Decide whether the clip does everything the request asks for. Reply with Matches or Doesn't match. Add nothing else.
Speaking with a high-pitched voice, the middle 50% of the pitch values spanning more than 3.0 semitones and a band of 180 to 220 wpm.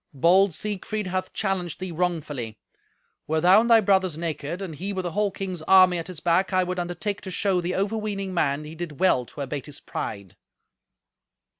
Doesn't match